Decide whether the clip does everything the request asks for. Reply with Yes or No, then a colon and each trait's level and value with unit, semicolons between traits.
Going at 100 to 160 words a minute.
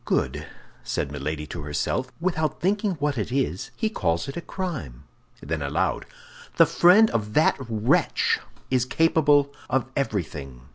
Yes: average, 145 wpm